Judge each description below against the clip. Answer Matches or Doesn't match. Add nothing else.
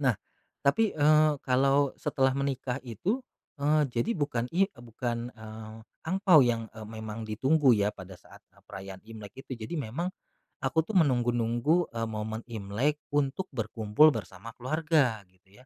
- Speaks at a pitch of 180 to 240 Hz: Doesn't match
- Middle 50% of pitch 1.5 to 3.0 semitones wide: Doesn't match